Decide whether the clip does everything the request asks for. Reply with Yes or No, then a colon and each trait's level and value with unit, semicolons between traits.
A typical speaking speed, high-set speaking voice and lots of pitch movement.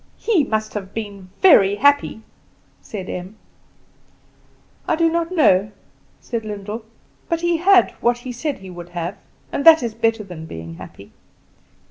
Yes: average, 150 wpm; high, 220 Hz; wide, 7.6 semitones